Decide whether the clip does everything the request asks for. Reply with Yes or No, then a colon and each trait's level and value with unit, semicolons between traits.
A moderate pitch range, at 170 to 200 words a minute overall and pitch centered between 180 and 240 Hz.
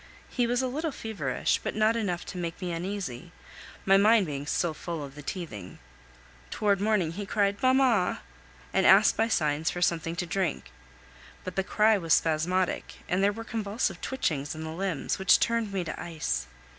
Yes: average, 4.7 semitones; average, 180 wpm; medium, 185 Hz